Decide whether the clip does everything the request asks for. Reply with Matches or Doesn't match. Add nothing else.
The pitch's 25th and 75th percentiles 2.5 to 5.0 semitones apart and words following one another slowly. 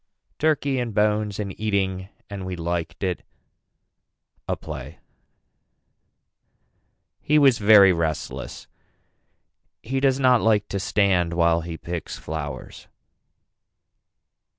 Matches